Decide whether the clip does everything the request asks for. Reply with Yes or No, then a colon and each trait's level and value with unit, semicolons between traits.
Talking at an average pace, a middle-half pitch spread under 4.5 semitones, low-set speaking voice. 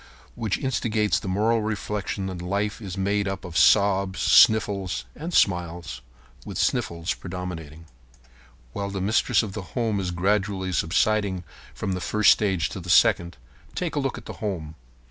Yes: average, 160 wpm; average, 2.8 semitones; very low, 95 Hz